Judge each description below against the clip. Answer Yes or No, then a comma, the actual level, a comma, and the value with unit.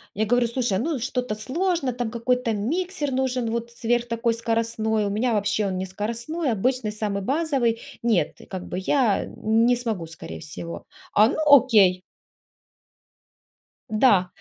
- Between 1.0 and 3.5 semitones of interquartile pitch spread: Yes, average, 3.2 semitones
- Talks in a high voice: Yes, high, 230 Hz